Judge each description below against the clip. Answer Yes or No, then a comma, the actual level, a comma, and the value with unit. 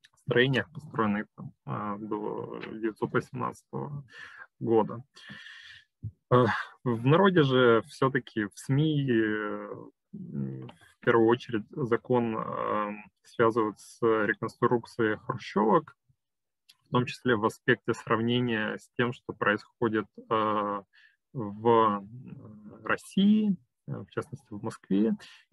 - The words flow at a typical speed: No, slow, 80 wpm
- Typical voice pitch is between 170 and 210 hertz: No, low, 115 Hz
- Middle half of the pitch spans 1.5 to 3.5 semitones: Yes, average, 3.1 semitones